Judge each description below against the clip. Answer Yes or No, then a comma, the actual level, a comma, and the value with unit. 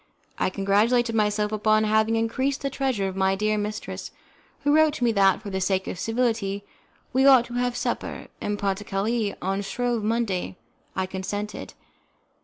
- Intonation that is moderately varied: Yes, average, 3.4 semitones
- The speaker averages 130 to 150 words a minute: No, average, 175 wpm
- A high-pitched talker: Yes, high, 215 Hz